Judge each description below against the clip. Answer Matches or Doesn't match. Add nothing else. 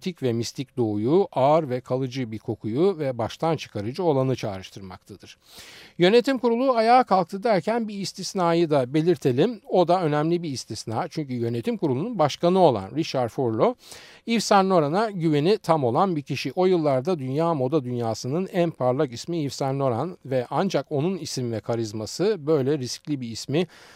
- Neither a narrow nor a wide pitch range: Doesn't match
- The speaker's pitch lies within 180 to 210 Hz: Doesn't match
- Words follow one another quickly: Matches